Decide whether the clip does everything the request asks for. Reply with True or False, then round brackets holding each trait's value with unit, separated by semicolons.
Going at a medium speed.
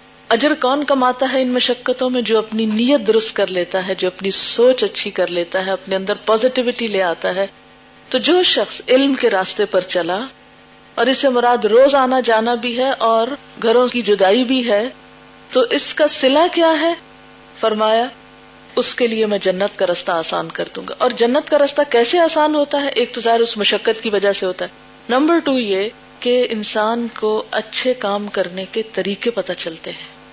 False (195 wpm)